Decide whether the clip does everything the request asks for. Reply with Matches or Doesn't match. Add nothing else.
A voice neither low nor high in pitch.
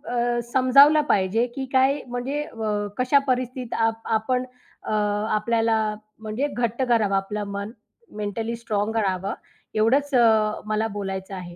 Doesn't match